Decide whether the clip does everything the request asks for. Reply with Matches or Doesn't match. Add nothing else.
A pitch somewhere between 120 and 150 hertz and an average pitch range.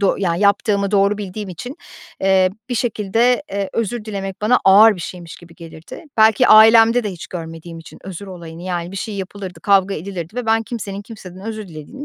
Doesn't match